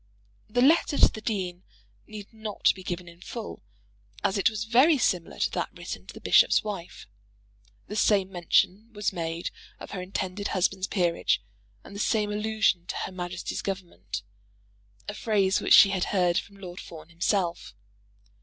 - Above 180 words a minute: No, average, 165 wpm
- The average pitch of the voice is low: No, high, 195 Hz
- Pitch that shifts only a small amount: No, average, 3.1 semitones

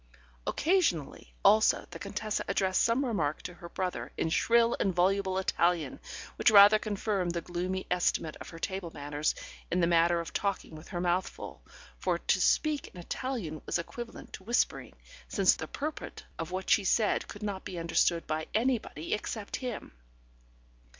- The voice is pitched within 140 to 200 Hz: Yes, medium, 185 Hz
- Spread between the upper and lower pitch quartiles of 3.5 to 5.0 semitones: Yes, average, 4.0 semitones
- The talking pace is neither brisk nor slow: Yes, average, 165 wpm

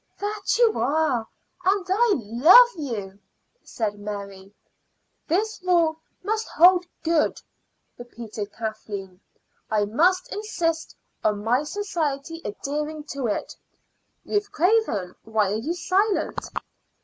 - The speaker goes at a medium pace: No, slow, 110 wpm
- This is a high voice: Yes, very high, 300 Hz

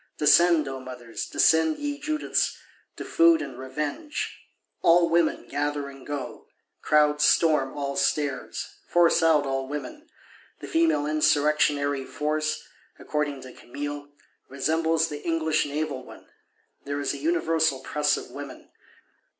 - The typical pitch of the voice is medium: Yes, medium, 150 Hz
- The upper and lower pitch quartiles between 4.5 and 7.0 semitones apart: No, narrow, 2.5 semitones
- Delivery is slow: Yes, slow, 125 wpm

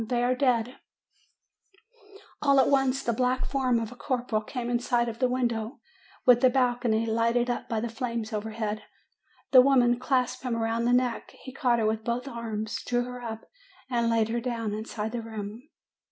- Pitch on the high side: Yes, high, 240 Hz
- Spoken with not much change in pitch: Yes, narrow, 2.0 semitones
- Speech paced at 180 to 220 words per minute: Yes, average, 190 wpm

